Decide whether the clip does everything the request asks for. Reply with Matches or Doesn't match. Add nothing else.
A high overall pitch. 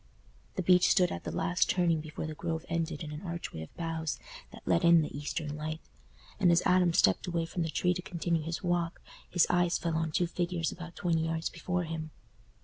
Doesn't match